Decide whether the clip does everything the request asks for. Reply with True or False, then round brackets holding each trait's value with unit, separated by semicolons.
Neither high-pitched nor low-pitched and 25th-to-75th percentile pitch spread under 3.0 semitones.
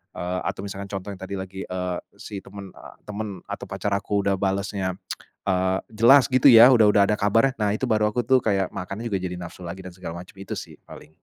False (100 Hz; 2.4 semitones)